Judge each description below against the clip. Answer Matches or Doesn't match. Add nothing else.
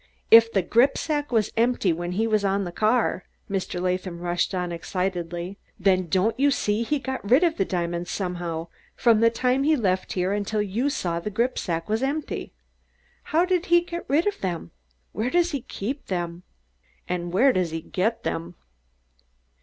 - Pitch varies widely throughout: Matches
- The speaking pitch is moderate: Doesn't match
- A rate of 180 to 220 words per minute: Matches